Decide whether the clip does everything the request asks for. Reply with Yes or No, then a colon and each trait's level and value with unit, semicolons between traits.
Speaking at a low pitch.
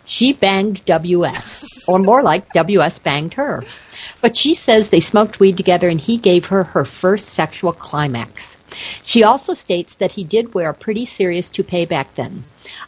No: high, 190 Hz